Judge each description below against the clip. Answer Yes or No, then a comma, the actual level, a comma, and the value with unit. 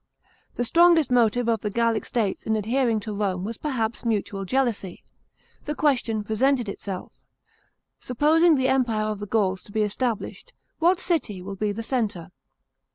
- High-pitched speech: Yes, high, 225 Hz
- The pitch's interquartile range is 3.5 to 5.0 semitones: Yes, average, 4.1 semitones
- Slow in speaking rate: No, average, 160 wpm